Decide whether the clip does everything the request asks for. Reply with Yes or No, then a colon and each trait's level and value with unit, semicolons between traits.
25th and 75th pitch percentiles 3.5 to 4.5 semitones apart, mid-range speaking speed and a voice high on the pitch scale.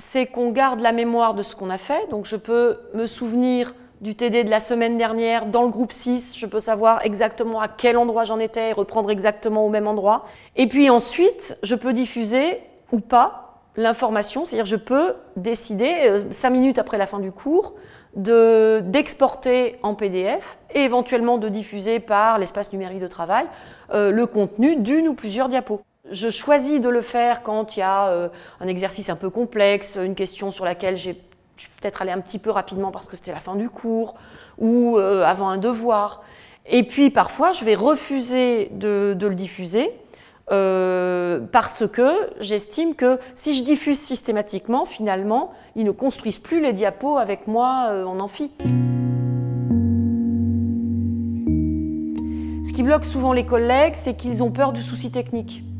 Yes: average, 4.1 semitones; average, 175 wpm; high, 220 Hz